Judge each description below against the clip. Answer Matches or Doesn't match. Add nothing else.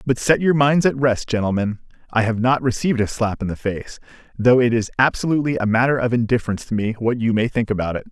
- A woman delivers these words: Doesn't match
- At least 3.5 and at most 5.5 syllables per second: Doesn't match